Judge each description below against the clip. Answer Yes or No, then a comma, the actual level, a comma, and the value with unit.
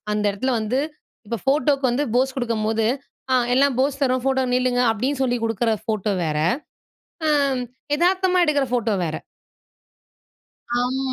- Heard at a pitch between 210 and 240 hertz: No, very high, 255 Hz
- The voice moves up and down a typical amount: Yes, average, 3.4 semitones